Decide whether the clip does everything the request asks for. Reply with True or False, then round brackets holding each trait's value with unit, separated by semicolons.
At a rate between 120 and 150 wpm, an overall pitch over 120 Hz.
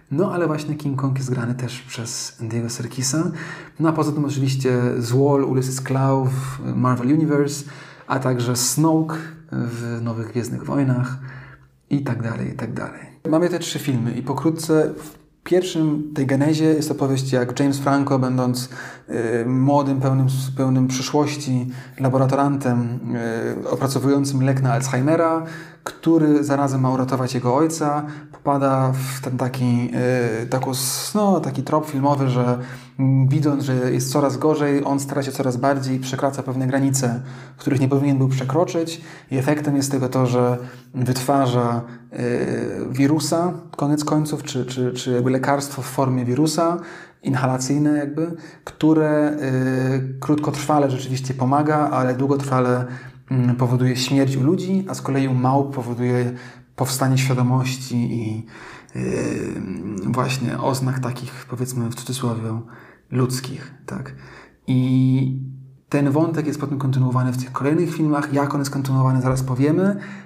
True (135 wpm; 135 Hz)